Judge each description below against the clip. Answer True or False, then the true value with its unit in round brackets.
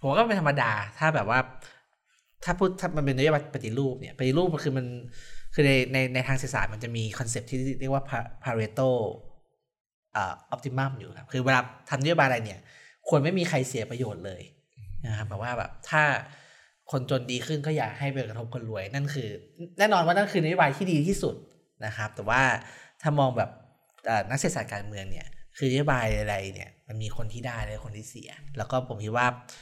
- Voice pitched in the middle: False (130 Hz)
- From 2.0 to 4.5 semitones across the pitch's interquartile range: True (3.8 semitones)